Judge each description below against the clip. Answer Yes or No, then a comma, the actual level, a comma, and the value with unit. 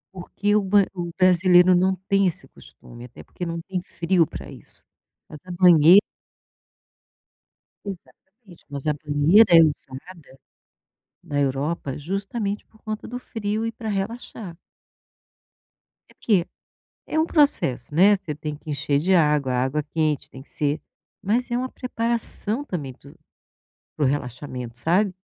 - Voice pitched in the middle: Yes, medium, 175 Hz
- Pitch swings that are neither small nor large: No, wide, 5.7 semitones